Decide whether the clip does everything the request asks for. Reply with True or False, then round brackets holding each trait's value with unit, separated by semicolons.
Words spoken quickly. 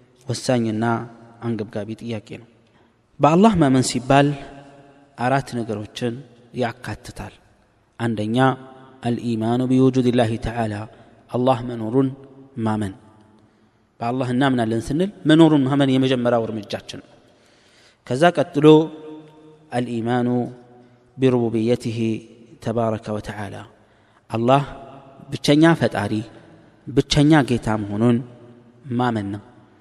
False (90 wpm)